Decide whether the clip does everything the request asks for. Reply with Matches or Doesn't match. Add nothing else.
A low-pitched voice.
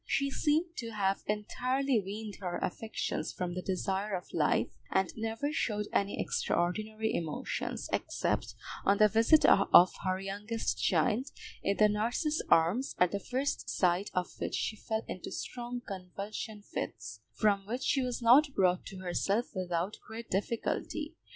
Doesn't match